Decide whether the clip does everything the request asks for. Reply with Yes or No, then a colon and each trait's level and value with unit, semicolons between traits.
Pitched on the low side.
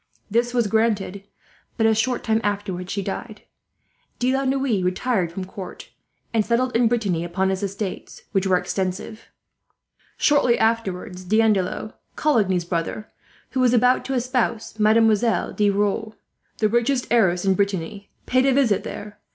No: high, 215 Hz